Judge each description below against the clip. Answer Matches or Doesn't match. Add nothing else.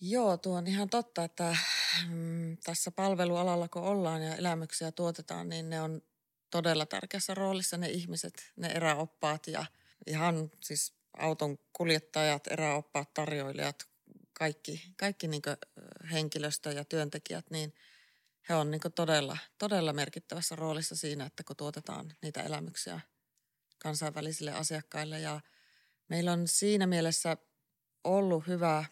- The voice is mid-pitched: Matches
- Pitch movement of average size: Doesn't match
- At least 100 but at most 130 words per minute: Matches